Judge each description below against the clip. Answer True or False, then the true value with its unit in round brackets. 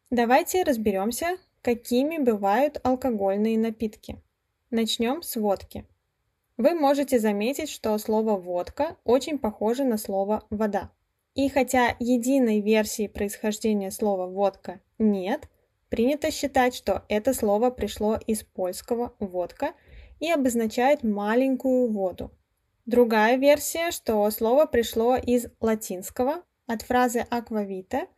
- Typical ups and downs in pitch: True (3.8 semitones)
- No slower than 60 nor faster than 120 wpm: True (110 wpm)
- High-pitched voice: True (230 Hz)